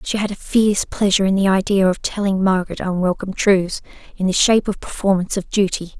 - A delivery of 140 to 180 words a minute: No, average, 200 wpm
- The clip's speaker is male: No, female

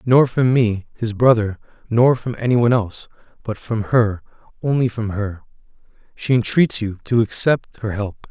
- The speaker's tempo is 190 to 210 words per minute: No, average, 165 wpm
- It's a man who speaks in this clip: Yes, male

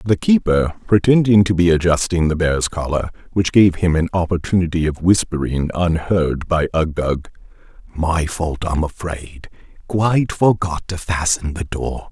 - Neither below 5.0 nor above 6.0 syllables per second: No, 4.5 syllables/s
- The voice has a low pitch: Yes, very low, 85 Hz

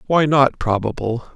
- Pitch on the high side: No, low, 125 Hz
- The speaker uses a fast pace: No, slow, 135 wpm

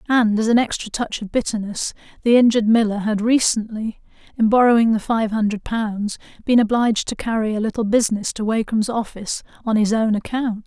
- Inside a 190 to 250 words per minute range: No, average, 180 wpm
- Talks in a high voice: Yes, high, 220 Hz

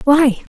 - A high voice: Yes, very high, 270 Hz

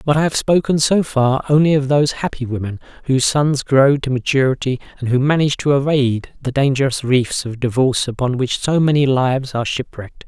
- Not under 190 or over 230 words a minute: Yes, average, 195 wpm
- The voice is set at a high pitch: No, low, 135 Hz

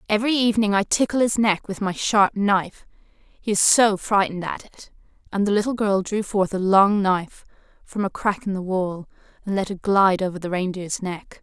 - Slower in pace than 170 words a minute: No, fast, 205 wpm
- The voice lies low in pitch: No, high, 200 Hz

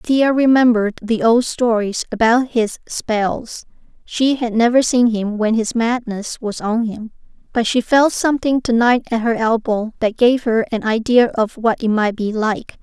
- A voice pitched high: Yes, high, 230 Hz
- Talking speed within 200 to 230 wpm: No, average, 180 wpm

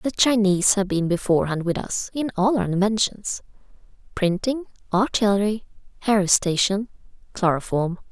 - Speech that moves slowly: Yes, slow, 105 wpm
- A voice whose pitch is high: Yes, high, 200 Hz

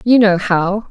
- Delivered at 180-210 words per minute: Yes, average, 200 wpm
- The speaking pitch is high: Yes, high, 200 Hz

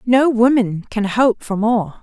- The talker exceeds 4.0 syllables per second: No, 3.7 syllables/s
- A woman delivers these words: Yes, female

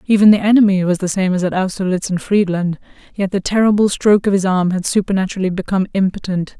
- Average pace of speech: Yes, average, 190 wpm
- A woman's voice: Yes, female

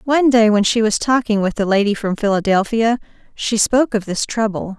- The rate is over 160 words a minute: Yes, average, 200 wpm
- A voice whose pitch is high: Yes, high, 220 Hz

